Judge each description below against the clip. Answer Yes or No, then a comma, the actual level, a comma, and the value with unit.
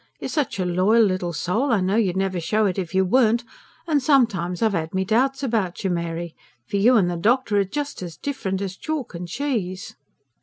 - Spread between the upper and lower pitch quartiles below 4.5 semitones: No, average, 5.0 semitones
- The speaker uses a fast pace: Yes, fast, 215 wpm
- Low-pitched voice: No, high, 195 Hz